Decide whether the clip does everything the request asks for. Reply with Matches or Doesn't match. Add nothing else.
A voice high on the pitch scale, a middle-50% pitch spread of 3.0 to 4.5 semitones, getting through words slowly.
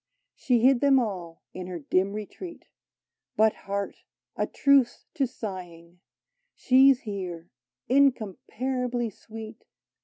Doesn't match